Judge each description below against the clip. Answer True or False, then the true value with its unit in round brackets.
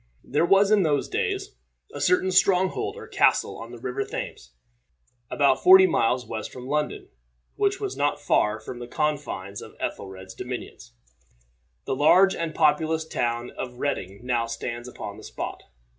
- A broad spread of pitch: True (7.4 semitones)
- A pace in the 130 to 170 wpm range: True (160 wpm)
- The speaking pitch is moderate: True (145 Hz)